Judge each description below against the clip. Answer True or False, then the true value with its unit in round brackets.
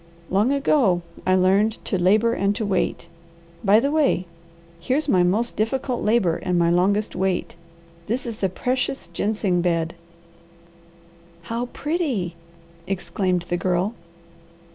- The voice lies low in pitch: False (200 Hz)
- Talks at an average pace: False (130 wpm)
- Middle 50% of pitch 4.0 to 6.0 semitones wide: True (4.7 semitones)